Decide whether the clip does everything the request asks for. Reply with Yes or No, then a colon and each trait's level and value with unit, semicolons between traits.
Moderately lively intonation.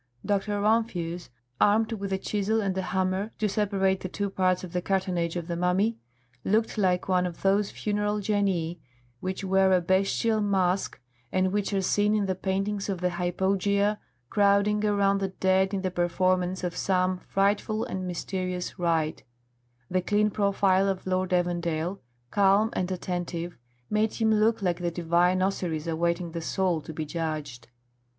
No: narrow, 2.2 semitones